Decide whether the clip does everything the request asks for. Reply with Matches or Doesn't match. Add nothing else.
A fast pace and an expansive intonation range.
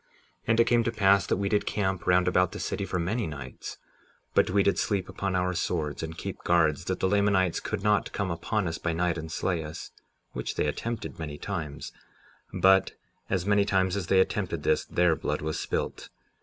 Doesn't match